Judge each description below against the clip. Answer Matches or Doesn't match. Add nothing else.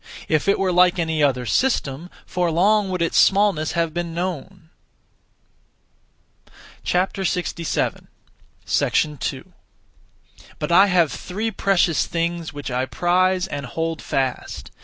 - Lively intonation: Doesn't match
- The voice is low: Doesn't match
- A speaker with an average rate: Doesn't match